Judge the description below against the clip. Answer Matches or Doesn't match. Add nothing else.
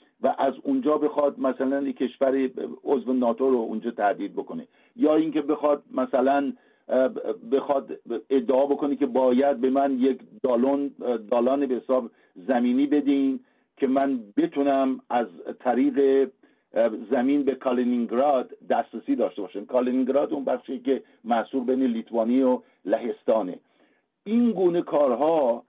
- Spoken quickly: Doesn't match